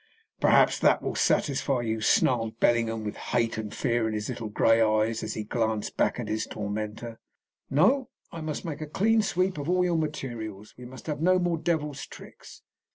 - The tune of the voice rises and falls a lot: Yes, wide, 6.1 semitones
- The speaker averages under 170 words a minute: No, average, 190 wpm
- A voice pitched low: Yes, low, 120 Hz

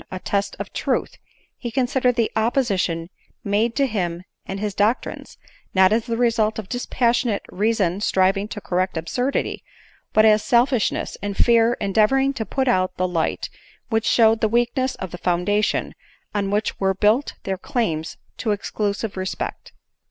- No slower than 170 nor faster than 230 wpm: No, average, 160 wpm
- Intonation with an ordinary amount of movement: Yes, average, 3.6 semitones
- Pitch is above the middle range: Yes, high, 215 Hz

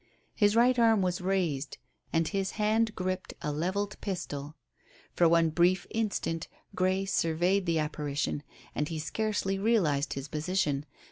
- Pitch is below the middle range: No, medium, 180 Hz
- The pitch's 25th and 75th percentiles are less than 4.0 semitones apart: No, average, 4.5 semitones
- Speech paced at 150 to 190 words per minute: No, average, 140 wpm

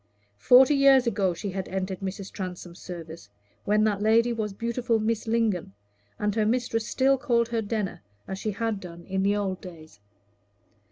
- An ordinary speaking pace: Yes, average, 170 wpm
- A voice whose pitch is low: No, high, 210 Hz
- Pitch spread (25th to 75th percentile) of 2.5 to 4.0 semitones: Yes, average, 3.5 semitones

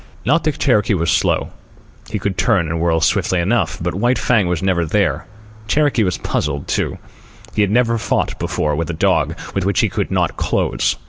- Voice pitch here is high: No, very low, 95 Hz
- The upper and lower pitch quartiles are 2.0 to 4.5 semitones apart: No, average, 5.3 semitones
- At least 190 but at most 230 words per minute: Yes, average, 195 wpm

